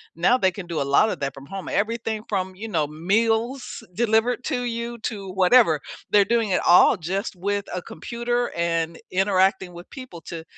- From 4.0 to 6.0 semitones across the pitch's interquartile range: Yes, average, 4.7 semitones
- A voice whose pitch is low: No, high, 195 Hz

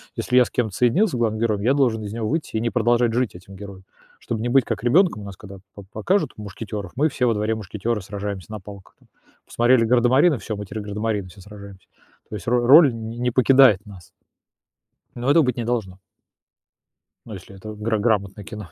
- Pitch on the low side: Yes, low, 110 Hz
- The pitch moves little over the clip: No, average, 3.2 semitones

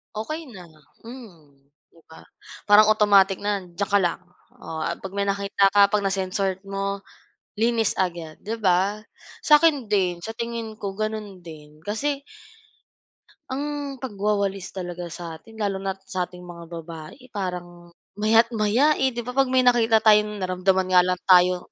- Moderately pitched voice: No, high, 200 Hz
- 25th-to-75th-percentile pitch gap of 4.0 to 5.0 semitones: No, average, 3.6 semitones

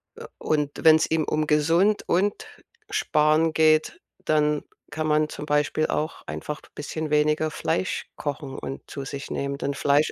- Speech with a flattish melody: Yes, narrow, 1.2 semitones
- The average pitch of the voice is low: No, medium, 155 Hz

